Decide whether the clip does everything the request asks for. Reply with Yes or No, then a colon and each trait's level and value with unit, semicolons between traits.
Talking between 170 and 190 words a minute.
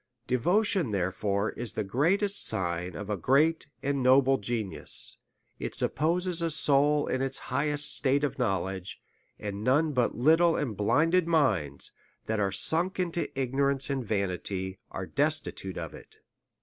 No: average, 150 wpm